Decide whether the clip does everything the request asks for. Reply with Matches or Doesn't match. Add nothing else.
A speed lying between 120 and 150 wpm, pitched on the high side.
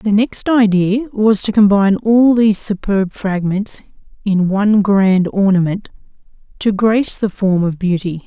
Matches